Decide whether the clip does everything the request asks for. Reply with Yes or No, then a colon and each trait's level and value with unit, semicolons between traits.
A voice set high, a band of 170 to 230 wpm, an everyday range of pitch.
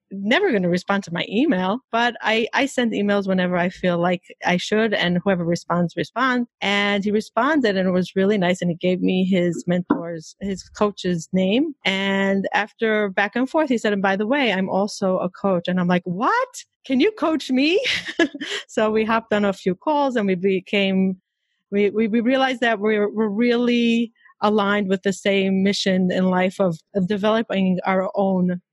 Yes: high, 200 Hz; average, 190 wpm; average, 3.7 semitones